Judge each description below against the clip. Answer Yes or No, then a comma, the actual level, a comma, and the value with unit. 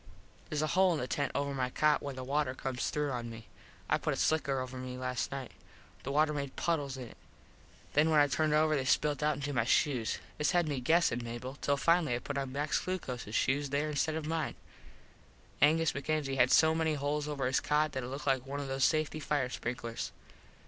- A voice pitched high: No, medium, 140 Hz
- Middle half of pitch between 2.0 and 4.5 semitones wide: Yes, average, 2.8 semitones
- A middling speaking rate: No, fast, 220 wpm